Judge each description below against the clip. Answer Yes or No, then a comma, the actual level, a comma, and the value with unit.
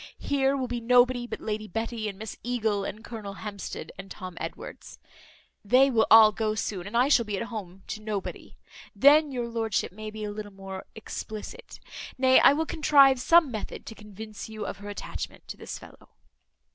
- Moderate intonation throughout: Yes, average, 3.1 semitones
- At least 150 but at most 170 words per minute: No, average, 190 wpm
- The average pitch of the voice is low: No, high, 220 Hz